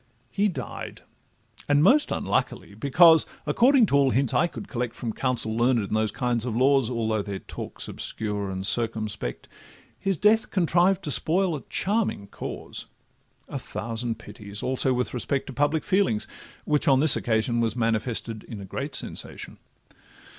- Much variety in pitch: Yes, wide, 5.9 semitones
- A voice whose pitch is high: No, low, 125 Hz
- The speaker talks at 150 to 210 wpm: Yes, average, 160 wpm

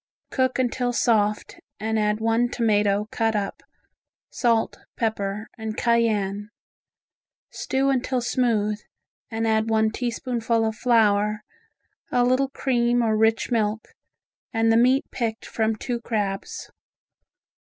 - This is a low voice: No, high, 225 Hz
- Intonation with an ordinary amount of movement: No, narrow, 2.1 semitones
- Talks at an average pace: No, slow, 120 wpm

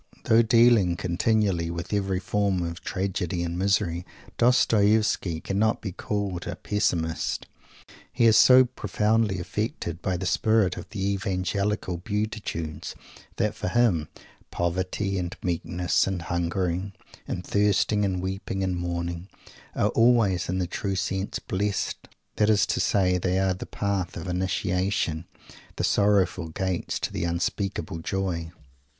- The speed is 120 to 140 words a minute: Yes, slow, 135 wpm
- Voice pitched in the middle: No, very low, 95 Hz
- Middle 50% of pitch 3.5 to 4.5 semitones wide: No, average, 2.9 semitones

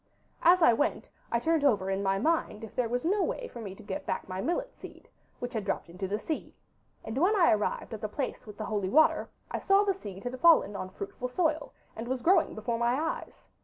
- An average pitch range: No, wide, 7.8 semitones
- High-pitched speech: Yes, high, 240 Hz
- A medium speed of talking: No, fast, 240 wpm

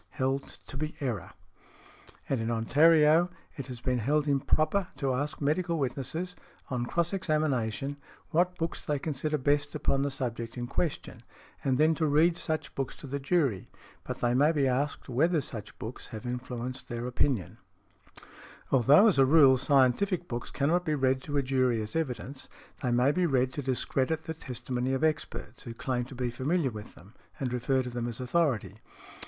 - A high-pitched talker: No, low, 135 Hz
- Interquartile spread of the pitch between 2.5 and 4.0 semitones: Yes, average, 3.7 semitones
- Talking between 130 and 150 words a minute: No, average, 180 wpm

